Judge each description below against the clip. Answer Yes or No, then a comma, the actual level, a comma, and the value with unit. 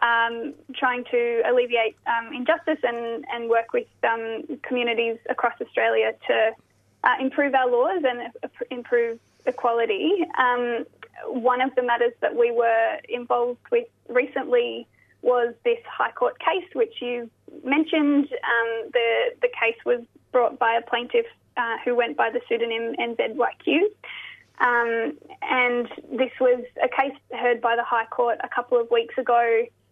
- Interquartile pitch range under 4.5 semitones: No, average, 5.0 semitones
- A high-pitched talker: Yes, high, 245 Hz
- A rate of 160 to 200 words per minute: No, average, 145 wpm